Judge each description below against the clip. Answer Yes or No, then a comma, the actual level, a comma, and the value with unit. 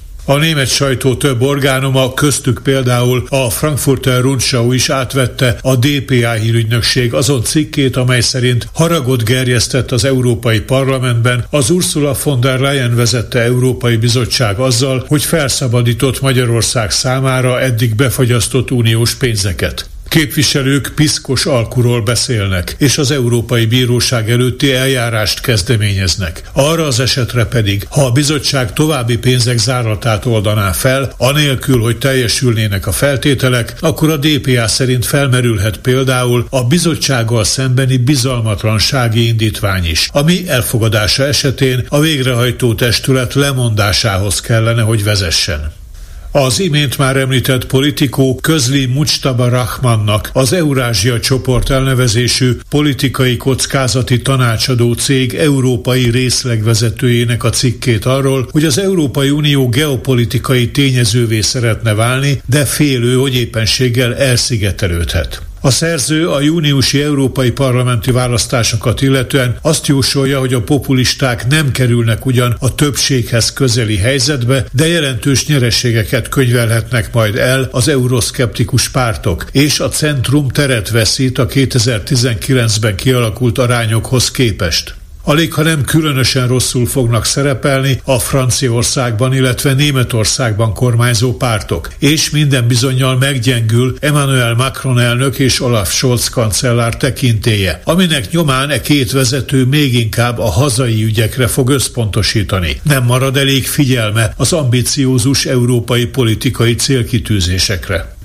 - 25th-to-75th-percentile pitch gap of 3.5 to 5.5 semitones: No, average, 2.7 semitones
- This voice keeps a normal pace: Yes, average, 115 wpm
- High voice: No, low, 125 Hz